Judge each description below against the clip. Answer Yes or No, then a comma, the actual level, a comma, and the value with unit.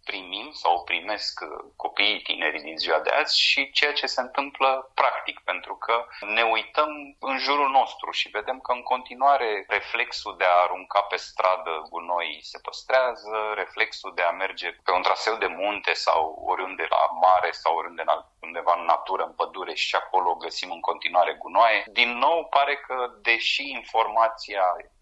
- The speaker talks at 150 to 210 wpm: Yes, fast, 170 wpm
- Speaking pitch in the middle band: No, low, 115 Hz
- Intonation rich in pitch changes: Yes, wide, 6.4 semitones